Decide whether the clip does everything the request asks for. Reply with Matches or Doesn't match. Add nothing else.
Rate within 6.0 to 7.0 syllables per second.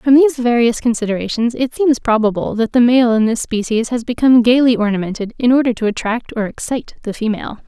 Matches